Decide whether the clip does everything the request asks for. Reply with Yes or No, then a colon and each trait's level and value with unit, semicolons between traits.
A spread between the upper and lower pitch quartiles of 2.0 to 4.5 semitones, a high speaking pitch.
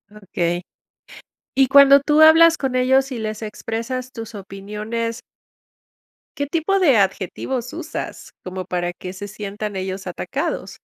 No: average, 5.3 semitones; high, 225 Hz